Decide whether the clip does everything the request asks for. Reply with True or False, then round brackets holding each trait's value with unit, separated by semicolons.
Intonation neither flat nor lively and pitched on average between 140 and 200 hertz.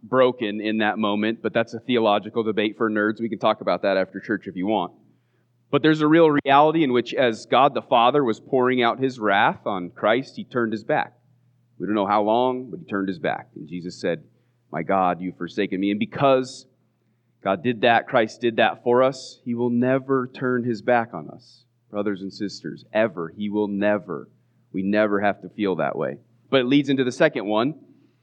False (3.4 semitones; 120 Hz)